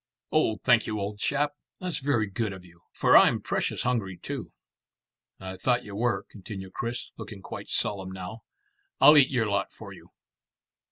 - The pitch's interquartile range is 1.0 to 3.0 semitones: No, average, 4.3 semitones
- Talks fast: No, average, 170 wpm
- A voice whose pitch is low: Yes, low, 110 Hz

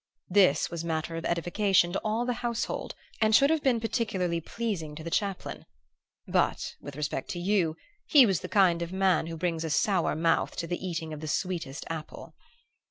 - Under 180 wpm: No, average, 190 wpm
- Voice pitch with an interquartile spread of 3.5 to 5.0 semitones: Yes, average, 4.2 semitones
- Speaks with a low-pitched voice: No, medium, 175 Hz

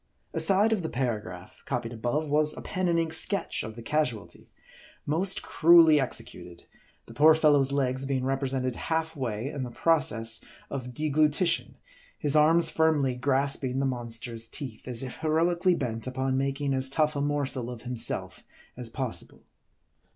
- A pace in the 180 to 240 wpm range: No, average, 160 wpm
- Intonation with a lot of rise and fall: No, average, 3.9 semitones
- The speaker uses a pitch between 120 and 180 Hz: Yes, low, 135 Hz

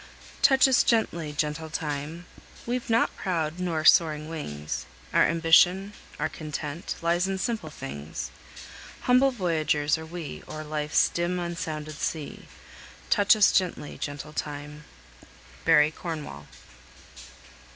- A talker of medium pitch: Yes, medium, 160 Hz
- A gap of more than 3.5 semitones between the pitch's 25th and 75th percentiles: No, average, 3.2 semitones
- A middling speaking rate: No, slow, 120 wpm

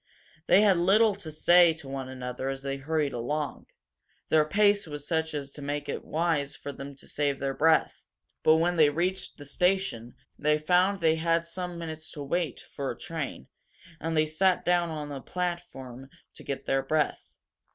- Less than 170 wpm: No, average, 185 wpm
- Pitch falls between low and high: Yes, medium, 155 Hz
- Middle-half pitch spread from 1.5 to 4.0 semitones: Yes, average, 3.7 semitones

